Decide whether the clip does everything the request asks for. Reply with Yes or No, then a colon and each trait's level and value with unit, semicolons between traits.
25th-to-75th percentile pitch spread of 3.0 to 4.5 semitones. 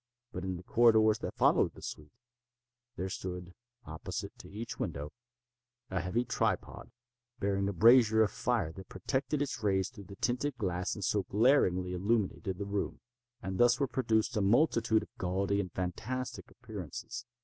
Yes: average, 4.1 semitones